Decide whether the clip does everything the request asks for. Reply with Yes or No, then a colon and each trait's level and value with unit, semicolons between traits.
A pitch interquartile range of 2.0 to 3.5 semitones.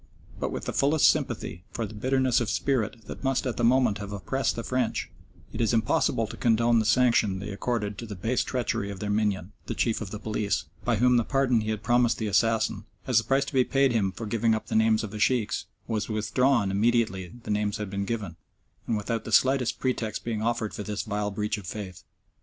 Yes: average, 2.7 semitones